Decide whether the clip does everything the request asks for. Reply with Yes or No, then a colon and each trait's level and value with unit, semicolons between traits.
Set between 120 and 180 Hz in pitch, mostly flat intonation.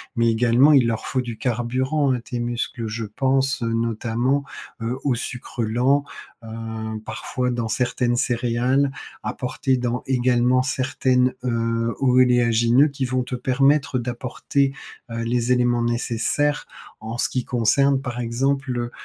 Yes: low, 125 Hz; narrow, 1.9 semitones